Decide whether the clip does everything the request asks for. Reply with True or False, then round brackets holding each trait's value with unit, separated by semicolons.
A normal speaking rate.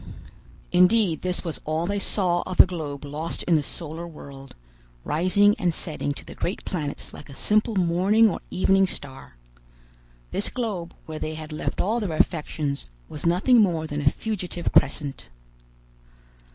True (160 wpm)